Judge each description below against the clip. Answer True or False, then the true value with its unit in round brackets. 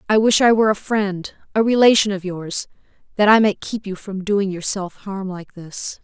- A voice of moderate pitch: False (200 Hz)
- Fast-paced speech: True (210 wpm)